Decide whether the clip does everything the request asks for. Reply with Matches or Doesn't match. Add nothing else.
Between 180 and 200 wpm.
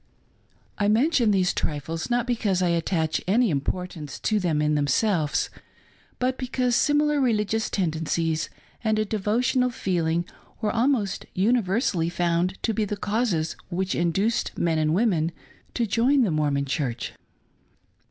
Doesn't match